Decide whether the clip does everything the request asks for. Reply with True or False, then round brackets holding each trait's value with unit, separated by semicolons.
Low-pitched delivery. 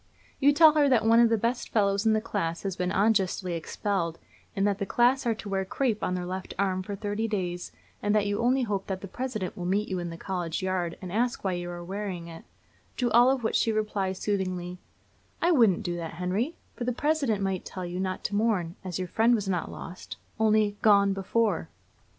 False (200 Hz)